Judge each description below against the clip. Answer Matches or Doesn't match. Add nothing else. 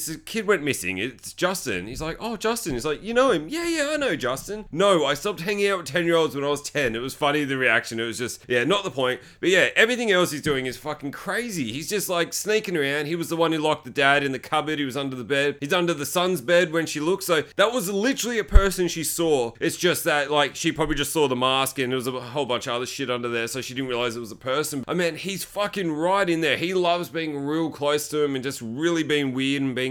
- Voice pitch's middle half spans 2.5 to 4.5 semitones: Doesn't match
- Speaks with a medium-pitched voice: Matches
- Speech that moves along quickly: Matches